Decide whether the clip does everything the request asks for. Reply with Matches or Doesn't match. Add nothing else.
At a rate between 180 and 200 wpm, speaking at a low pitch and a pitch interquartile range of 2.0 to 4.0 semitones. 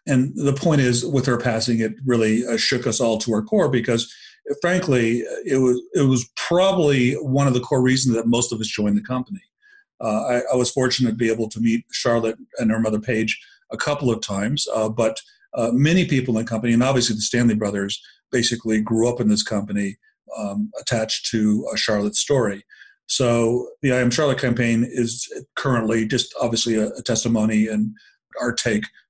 Matches